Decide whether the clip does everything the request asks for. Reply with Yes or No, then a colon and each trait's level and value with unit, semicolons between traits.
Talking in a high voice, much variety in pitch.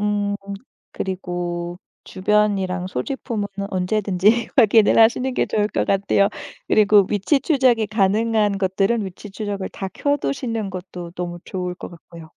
No: high, 200 Hz; average, 2.9 semitones